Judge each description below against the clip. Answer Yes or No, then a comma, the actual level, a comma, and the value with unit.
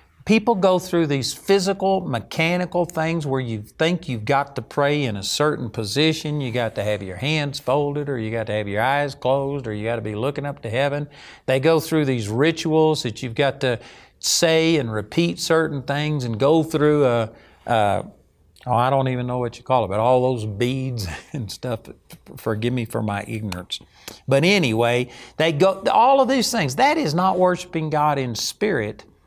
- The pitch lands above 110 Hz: Yes, medium, 140 Hz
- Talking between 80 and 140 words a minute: No, average, 195 wpm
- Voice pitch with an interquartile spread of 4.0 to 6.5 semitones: Yes, average, 5.2 semitones